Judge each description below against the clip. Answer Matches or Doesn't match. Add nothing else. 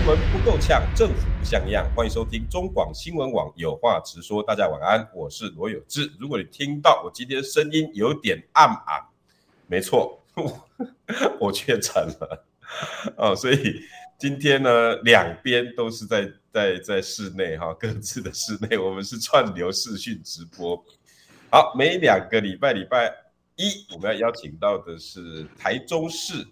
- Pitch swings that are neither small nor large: Doesn't match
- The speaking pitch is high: Doesn't match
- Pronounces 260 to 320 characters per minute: Doesn't match